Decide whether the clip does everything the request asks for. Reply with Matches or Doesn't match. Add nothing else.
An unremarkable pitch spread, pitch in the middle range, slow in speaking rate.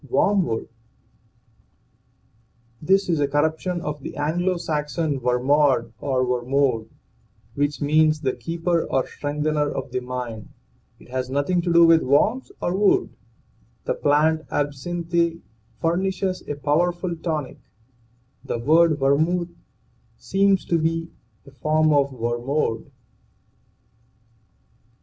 Matches